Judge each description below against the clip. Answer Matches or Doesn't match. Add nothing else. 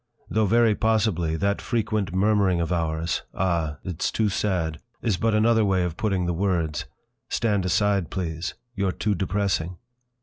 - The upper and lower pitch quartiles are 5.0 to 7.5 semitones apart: Doesn't match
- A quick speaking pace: Doesn't match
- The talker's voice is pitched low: Matches